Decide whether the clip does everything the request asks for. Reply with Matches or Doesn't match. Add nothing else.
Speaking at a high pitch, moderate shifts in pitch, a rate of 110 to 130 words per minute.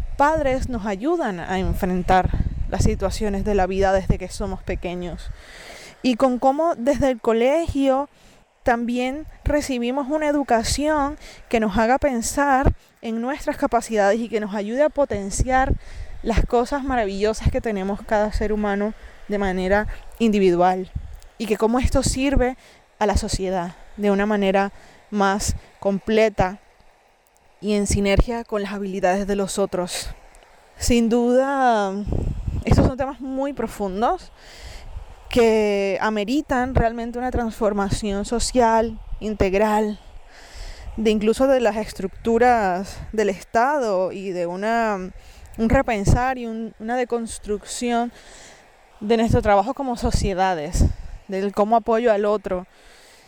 Matches